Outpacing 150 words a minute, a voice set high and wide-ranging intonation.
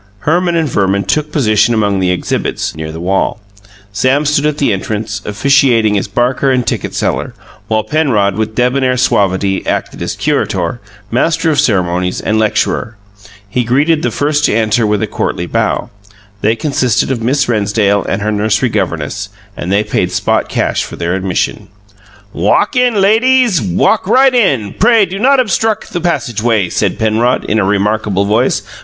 No: average, 170 wpm; low, 115 Hz; wide, 6.6 semitones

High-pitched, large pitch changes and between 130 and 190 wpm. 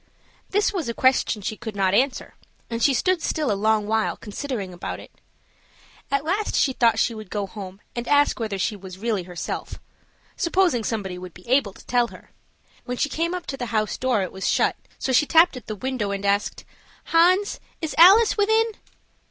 No: high, 235 Hz; wide, 7.0 semitones; average, 200 wpm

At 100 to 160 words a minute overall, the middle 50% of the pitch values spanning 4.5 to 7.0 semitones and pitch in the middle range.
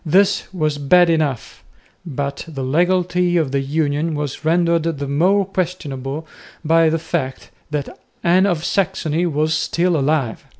No: average, 140 wpm; average, 3.5 semitones; medium, 160 Hz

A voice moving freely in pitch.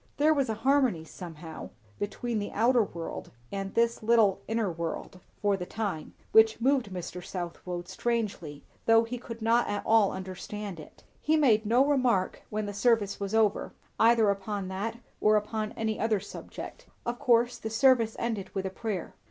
No: average, 3.4 semitones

